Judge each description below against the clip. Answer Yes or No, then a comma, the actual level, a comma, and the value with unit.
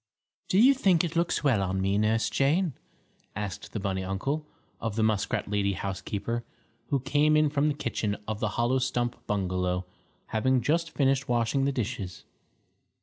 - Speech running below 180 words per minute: Yes, average, 165 wpm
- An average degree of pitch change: No, wide, 6.0 semitones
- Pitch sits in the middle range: No, low, 120 Hz